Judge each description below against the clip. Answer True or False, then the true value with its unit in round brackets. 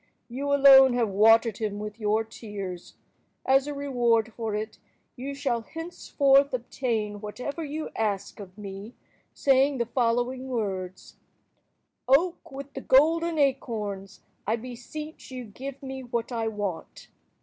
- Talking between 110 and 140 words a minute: True (135 wpm)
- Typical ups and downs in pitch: True (4.3 semitones)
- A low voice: False (240 Hz)